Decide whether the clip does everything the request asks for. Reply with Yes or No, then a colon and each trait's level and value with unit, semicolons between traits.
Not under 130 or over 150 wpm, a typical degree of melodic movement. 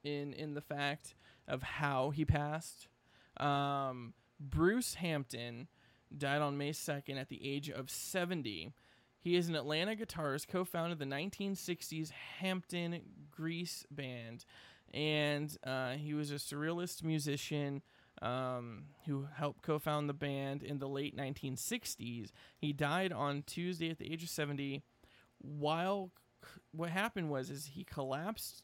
Yes: slow, 135 wpm; average, 3.1 semitones